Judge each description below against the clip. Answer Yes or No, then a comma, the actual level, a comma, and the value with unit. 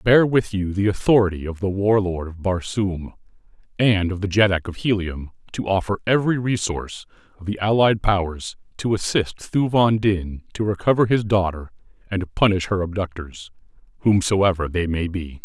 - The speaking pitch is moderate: No, very low, 95 Hz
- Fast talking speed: No, average, 155 wpm